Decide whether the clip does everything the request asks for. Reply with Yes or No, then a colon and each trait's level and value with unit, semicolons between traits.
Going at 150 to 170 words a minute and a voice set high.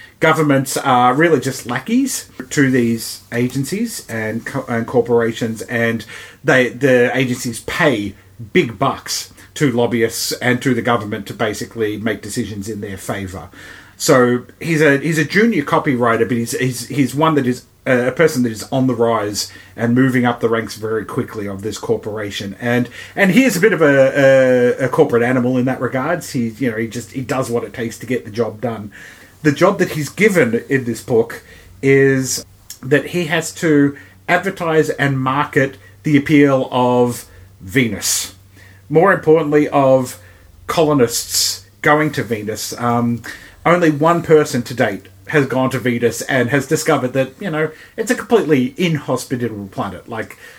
No: average, 165 wpm; low, 125 Hz